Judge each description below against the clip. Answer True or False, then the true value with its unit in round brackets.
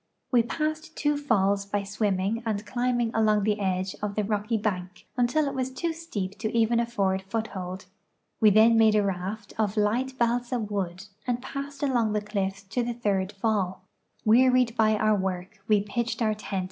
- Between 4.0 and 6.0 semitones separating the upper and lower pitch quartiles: False (3.2 semitones)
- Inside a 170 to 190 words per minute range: True (180 wpm)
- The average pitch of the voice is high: True (215 Hz)